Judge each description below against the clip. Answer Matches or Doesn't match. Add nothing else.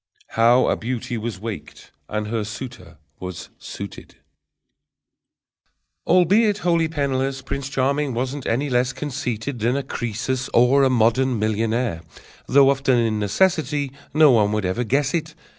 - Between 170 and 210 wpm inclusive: Doesn't match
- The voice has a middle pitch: Doesn't match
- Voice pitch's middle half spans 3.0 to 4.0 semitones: Matches